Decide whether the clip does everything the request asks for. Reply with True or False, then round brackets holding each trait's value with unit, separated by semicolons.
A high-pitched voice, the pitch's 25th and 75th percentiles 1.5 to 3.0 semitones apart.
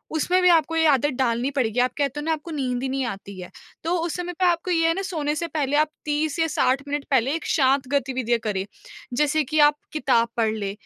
False (285 Hz; 4.2 semitones)